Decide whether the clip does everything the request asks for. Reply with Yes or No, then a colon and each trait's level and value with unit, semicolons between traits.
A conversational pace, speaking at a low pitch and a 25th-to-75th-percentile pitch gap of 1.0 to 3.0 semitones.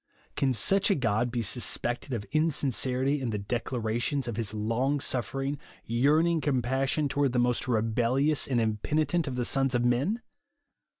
No: average, 160 wpm; low, 130 Hz; average, 3.5 semitones